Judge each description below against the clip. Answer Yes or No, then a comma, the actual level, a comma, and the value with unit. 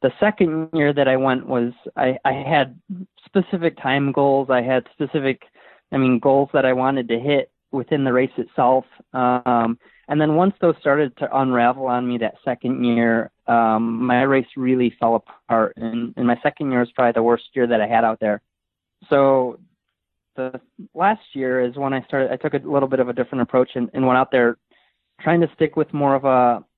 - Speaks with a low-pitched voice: Yes, low, 130 Hz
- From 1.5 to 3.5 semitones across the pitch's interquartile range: Yes, average, 2.8 semitones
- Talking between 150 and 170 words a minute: No, fast, 205 wpm